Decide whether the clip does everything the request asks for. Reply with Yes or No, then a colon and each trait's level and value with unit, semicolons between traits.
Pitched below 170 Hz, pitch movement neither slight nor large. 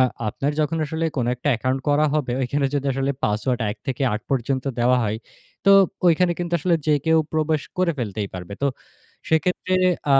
Yes: medium, 140 Hz; average, 4.4 semitones